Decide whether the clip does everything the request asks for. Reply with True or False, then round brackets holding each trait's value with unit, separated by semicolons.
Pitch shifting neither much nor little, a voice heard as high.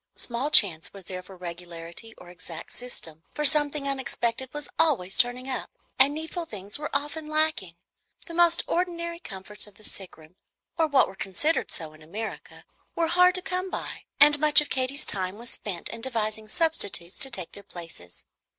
False (8.4 semitones; 240 Hz)